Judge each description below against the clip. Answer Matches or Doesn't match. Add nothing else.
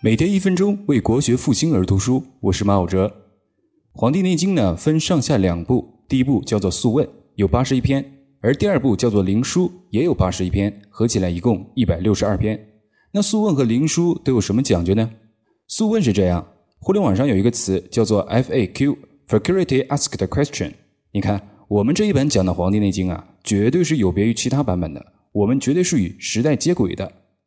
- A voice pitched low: Matches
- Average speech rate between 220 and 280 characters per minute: Doesn't match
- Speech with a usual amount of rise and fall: Doesn't match